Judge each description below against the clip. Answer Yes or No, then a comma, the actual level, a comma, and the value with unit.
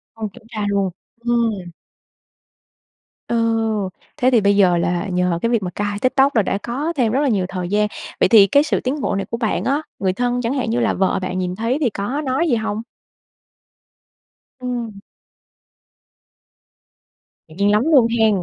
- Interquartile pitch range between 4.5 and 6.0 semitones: No, average, 3.8 semitones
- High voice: Yes, high, 220 Hz